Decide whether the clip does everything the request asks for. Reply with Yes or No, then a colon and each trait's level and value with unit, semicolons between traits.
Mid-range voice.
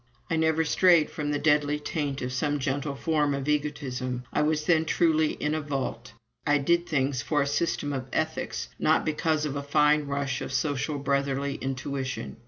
Yes: medium, 145 Hz